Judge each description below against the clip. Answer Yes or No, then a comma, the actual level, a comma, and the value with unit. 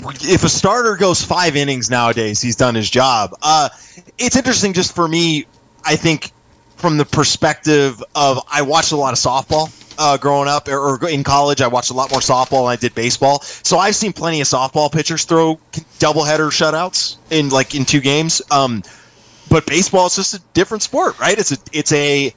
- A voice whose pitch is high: No, medium, 145 Hz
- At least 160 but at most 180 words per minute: No, average, 200 wpm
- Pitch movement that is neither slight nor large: Yes, average, 3.6 semitones